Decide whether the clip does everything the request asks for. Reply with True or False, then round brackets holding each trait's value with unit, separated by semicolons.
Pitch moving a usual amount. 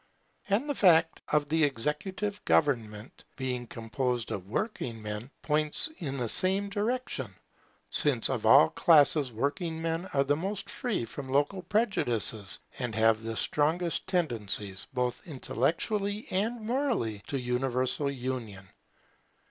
False (7.7 semitones)